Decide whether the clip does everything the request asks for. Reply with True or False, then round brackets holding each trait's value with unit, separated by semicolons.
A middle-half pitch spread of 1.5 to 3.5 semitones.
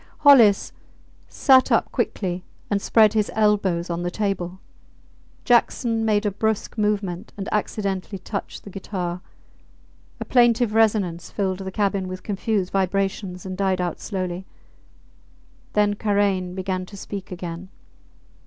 True (2.4 semitones)